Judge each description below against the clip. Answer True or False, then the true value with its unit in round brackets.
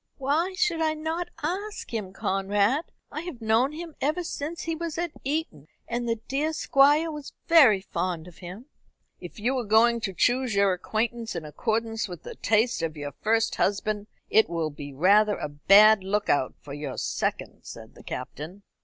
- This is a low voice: False (225 Hz)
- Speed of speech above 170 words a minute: True (180 wpm)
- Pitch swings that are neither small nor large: False (7.8 semitones)